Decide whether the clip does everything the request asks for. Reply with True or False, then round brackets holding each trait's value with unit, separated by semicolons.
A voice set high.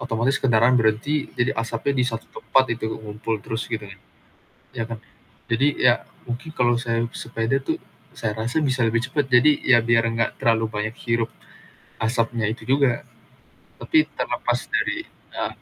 False (115 Hz)